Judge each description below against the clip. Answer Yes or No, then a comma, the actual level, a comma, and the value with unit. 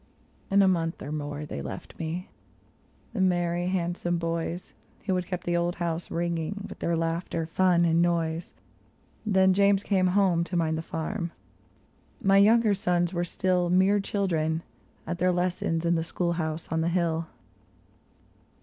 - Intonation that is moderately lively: No, narrow, 2.1 semitones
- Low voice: No, medium, 175 Hz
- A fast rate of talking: No, average, 165 wpm